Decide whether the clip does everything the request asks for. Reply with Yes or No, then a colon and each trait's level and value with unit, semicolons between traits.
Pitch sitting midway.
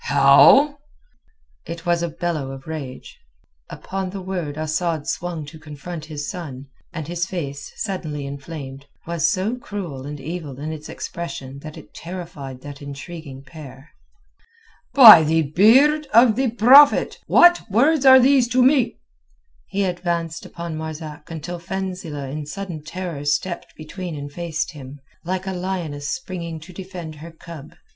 Yes: medium, 165 Hz